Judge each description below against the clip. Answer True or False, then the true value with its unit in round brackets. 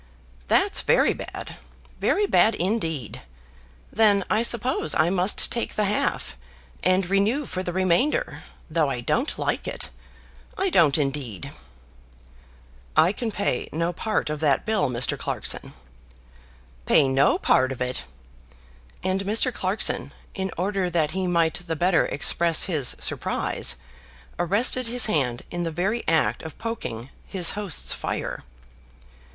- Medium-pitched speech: True (180 Hz)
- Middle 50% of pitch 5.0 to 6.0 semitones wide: True (5.5 semitones)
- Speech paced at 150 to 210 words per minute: False (135 wpm)